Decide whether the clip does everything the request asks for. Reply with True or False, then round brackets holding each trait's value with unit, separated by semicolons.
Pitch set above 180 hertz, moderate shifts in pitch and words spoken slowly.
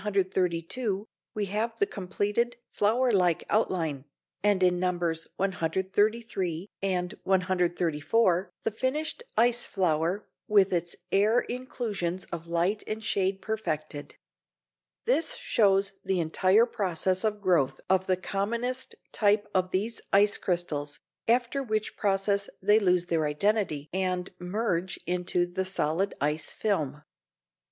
True (190 Hz; 3.3 semitones; 120 wpm)